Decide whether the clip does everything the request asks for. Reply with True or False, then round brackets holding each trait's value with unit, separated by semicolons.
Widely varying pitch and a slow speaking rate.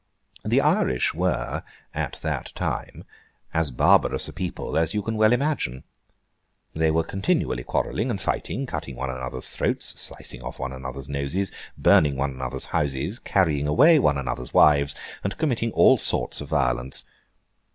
False (6.8 semitones; 150 wpm)